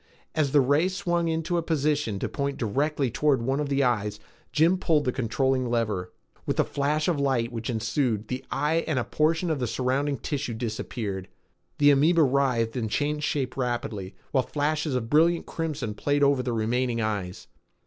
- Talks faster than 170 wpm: Yes, average, 180 wpm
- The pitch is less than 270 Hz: Yes, low, 135 Hz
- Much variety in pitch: No, average, 4.4 semitones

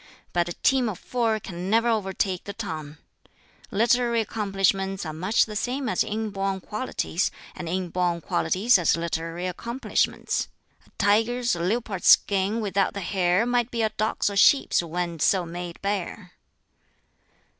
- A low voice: No, high, 195 Hz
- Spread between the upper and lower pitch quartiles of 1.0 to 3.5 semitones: No, average, 4.0 semitones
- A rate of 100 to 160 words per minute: Yes, average, 150 wpm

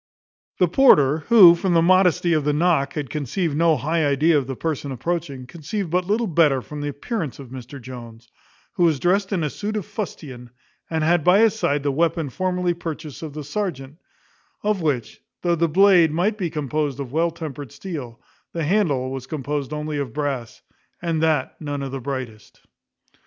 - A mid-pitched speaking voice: Yes, medium, 155 Hz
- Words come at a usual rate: Yes, average, 190 wpm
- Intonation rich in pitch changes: No, average, 4.0 semitones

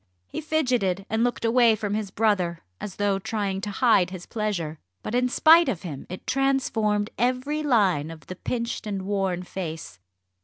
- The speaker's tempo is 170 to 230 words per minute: Yes, average, 175 wpm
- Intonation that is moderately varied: Yes, average, 4.7 semitones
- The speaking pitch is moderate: No, high, 210 Hz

